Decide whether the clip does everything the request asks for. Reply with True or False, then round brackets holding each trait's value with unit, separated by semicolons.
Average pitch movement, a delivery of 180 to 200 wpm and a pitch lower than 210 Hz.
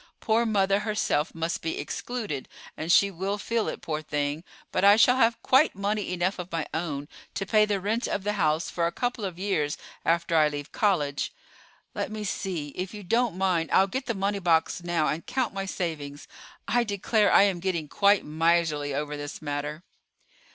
True (4.8 semitones; 195 wpm; 185 Hz)